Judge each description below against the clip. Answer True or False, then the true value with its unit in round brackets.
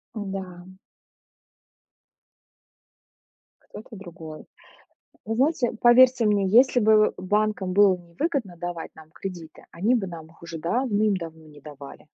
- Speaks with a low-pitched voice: False (190 Hz)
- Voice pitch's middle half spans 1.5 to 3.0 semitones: False (4.5 semitones)